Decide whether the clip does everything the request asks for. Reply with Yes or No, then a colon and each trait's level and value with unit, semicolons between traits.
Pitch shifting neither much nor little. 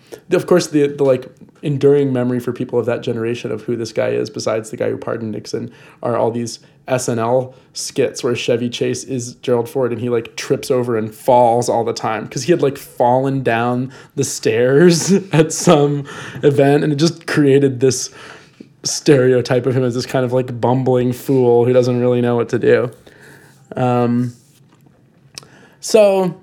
Yes: average, 3.0 semitones